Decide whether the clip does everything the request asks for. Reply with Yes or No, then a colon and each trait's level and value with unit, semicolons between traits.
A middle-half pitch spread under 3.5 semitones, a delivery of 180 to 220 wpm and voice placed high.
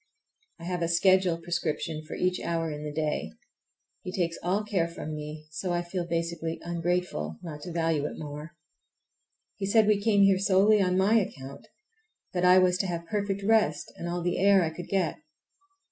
No: average, 2.7 semitones; average, 190 wpm; medium, 175 Hz